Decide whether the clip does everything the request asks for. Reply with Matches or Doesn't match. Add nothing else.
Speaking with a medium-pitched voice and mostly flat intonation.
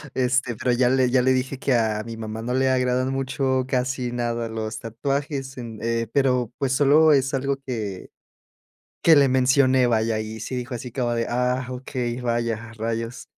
Doesn't match